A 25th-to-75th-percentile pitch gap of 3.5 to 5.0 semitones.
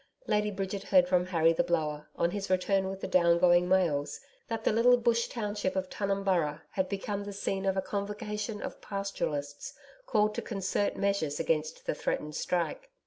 No: average, 3.0 semitones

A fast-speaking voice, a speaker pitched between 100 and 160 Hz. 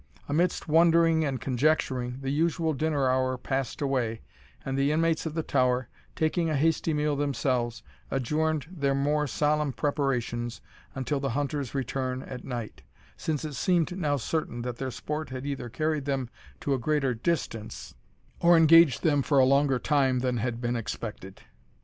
No: average, 165 wpm; medium, 140 Hz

